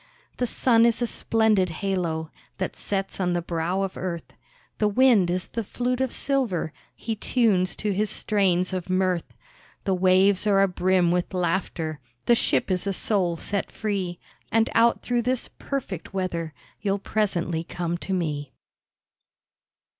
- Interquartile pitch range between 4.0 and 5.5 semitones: No, average, 3.5 semitones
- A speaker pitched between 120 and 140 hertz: No, high, 190 Hz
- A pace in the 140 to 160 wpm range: Yes, average, 155 wpm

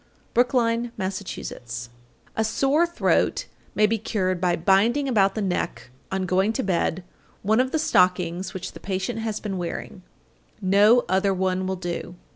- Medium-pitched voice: No, high, 195 Hz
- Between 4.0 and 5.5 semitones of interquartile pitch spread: No, average, 3.5 semitones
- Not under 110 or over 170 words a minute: Yes, average, 160 wpm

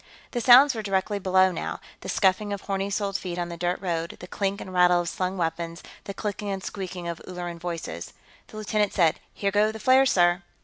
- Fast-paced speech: Yes, fast, 215 wpm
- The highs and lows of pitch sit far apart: No, average, 2.7 semitones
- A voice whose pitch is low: No, high, 190 Hz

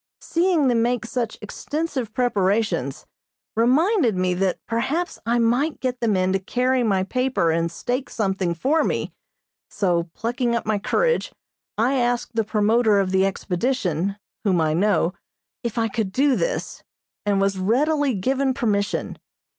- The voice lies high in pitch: Yes, high, 230 Hz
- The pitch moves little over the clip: No, average, 4.9 semitones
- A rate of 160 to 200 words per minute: No, average, 150 wpm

